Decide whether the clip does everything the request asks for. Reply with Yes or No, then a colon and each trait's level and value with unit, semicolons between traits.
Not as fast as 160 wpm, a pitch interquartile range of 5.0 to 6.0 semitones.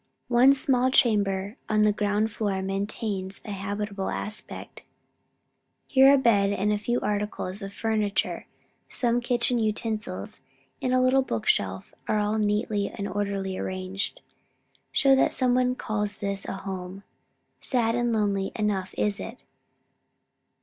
No: slow, 135 wpm; average, 3.2 semitones